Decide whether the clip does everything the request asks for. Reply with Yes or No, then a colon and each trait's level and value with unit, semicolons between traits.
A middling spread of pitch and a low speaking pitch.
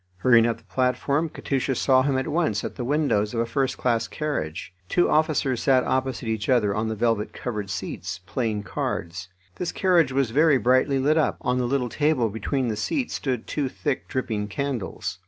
Yes: average, 4.0 semitones; low, 125 Hz